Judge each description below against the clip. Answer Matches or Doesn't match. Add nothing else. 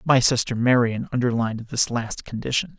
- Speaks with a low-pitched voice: Matches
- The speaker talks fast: Doesn't match